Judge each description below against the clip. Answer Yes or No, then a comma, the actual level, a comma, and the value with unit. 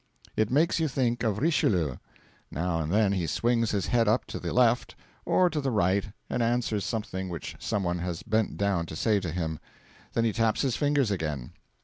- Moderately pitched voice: No, low, 105 Hz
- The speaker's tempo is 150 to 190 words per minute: No, fast, 205 wpm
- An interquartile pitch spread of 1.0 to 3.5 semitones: No, average, 5.3 semitones